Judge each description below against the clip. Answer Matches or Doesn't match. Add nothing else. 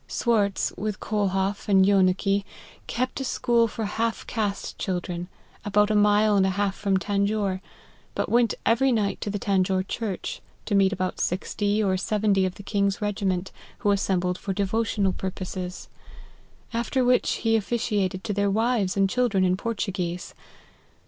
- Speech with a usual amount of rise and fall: Doesn't match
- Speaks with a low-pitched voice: Doesn't match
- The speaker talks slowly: Doesn't match